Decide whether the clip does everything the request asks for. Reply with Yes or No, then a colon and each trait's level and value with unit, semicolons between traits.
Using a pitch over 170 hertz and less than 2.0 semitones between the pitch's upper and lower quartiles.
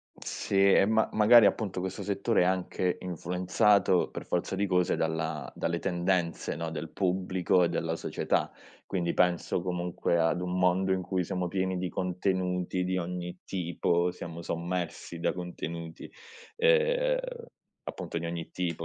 No: very low, 90 Hz; narrow, 1.6 semitones